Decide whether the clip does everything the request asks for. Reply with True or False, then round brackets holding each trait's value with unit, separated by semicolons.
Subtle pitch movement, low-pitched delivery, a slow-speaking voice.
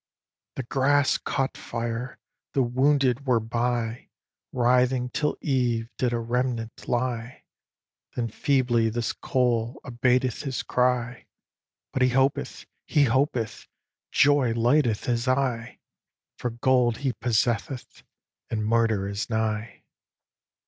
True (2.0 semitones; 125 Hz; 115 wpm)